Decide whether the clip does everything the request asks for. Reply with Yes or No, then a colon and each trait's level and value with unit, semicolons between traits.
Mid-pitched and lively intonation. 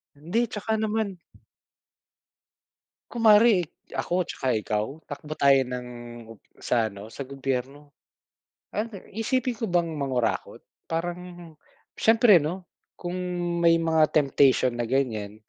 Yes: medium, 160 Hz; wide, 6.3 semitones